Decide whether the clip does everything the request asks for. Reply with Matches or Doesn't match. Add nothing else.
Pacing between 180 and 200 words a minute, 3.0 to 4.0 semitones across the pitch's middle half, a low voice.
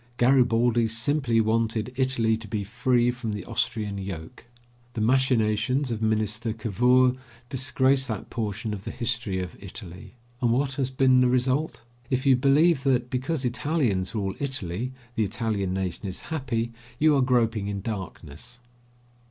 Doesn't match